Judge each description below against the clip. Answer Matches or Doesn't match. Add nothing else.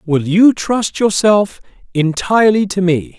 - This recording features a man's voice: Matches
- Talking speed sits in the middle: Doesn't match